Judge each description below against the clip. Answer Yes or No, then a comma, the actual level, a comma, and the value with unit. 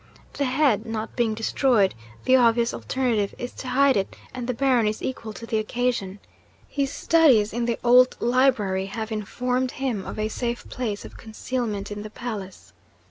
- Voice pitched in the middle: No, high, 235 Hz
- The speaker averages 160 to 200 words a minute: Yes, average, 175 wpm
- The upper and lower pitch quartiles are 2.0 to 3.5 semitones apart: Yes, average, 2.9 semitones